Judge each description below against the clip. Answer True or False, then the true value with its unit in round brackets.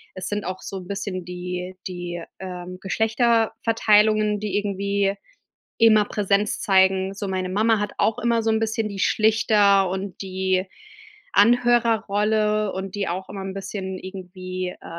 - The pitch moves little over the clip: True (2.3 semitones)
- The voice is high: True (200 Hz)